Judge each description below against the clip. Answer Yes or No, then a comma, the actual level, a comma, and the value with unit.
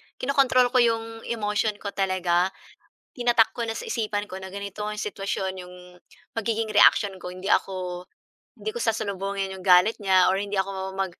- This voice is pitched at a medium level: No, high, 200 Hz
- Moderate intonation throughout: Yes, average, 3.0 semitones